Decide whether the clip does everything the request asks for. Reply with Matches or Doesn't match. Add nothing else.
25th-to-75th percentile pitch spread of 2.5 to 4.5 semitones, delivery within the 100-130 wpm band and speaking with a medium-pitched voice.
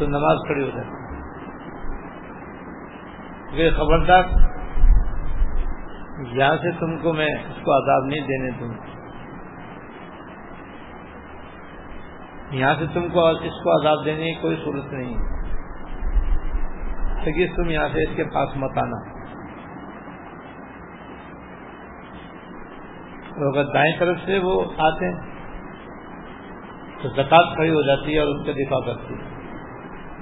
Matches